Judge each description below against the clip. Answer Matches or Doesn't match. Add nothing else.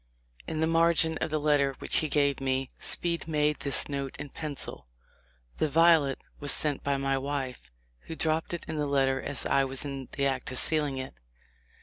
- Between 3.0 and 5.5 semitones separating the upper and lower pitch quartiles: Doesn't match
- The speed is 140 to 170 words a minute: Doesn't match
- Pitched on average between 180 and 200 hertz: Doesn't match